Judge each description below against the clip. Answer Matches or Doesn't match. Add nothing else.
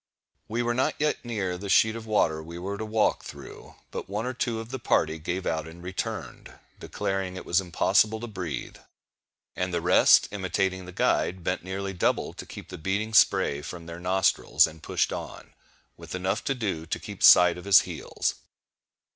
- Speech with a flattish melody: Doesn't match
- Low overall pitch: Matches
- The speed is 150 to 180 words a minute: Doesn't match